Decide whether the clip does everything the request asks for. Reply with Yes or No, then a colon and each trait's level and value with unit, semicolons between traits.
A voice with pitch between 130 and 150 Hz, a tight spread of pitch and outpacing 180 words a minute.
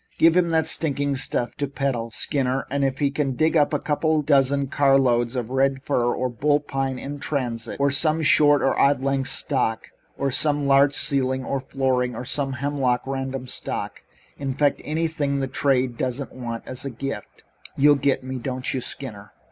Yes: low, 135 Hz; narrow, 1.9 semitones; average, 190 wpm